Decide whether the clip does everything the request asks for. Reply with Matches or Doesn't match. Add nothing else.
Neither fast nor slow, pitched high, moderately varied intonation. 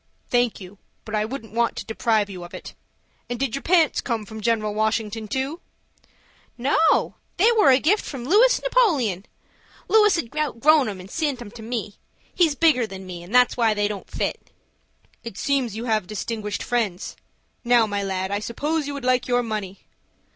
Matches